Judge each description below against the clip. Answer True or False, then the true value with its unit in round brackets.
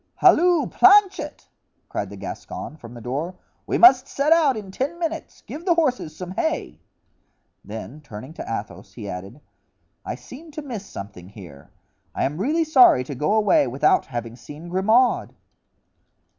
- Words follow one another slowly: False (155 wpm)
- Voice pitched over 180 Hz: True (190 Hz)